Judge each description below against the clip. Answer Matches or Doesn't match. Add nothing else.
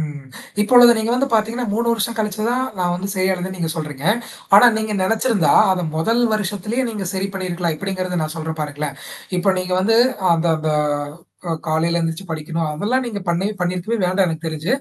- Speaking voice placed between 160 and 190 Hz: Matches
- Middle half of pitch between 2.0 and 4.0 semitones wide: Doesn't match